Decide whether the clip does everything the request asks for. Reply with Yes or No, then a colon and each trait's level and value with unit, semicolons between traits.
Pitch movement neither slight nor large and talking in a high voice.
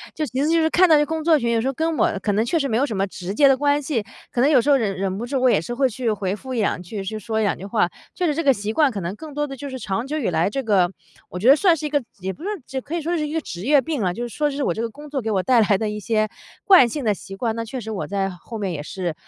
No: wide, 6.1 semitones; high, 240 Hz